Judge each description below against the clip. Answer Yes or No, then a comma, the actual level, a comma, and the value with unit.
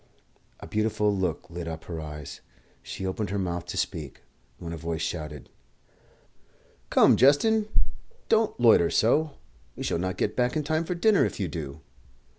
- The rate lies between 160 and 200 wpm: Yes, average, 165 wpm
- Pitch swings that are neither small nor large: No, wide, 8.8 semitones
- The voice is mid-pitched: No, very low, 95 Hz